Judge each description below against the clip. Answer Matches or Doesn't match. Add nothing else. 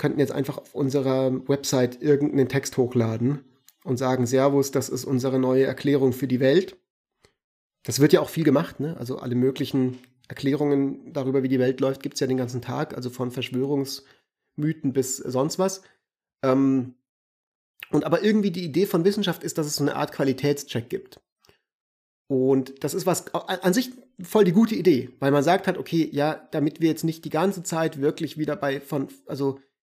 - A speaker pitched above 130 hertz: Matches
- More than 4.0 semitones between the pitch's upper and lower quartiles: Doesn't match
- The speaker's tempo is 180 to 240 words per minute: Matches